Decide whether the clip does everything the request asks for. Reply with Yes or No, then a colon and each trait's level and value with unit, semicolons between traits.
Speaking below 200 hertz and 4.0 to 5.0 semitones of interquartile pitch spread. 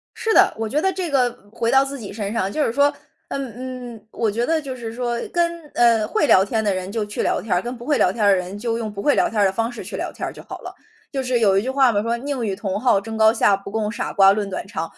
No: high, 230 Hz; average, 4.3 semitones